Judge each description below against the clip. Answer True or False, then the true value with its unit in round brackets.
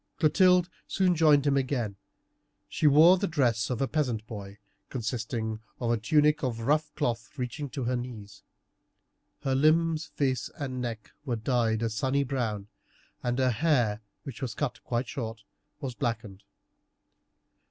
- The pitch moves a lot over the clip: False (4.5 semitones)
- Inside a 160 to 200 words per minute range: False (150 wpm)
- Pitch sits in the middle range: False (125 Hz)